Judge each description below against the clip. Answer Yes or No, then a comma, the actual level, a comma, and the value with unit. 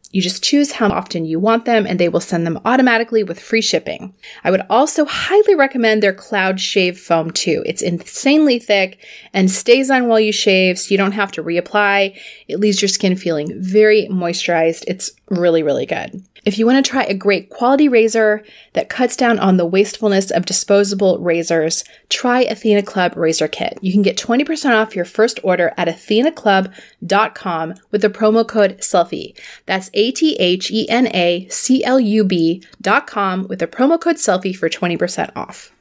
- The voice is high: Yes, high, 205 Hz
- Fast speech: No, average, 180 wpm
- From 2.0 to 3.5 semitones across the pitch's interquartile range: No, average, 4.0 semitones